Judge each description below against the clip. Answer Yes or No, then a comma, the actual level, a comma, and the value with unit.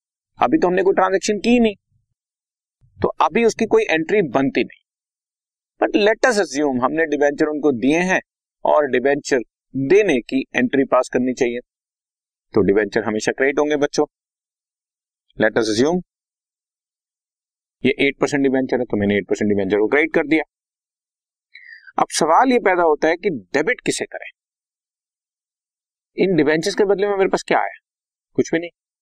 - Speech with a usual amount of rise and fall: No, wide, 6.6 semitones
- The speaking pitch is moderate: Yes, medium, 155 Hz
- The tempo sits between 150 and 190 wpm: Yes, average, 155 wpm